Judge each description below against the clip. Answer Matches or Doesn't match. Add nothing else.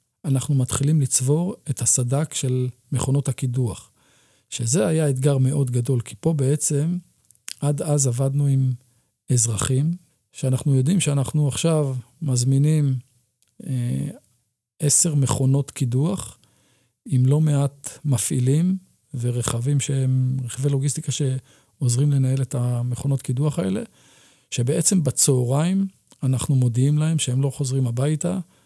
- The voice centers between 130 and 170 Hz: Matches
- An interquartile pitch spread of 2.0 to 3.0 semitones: Matches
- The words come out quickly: Doesn't match